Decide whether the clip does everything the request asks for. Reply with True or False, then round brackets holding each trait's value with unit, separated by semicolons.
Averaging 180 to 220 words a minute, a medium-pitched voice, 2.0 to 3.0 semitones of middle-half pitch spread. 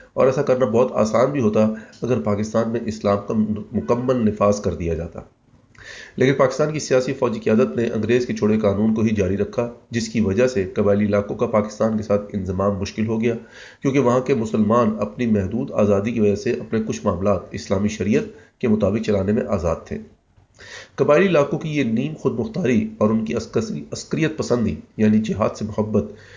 False (190 wpm; 110 Hz; 2.6 semitones)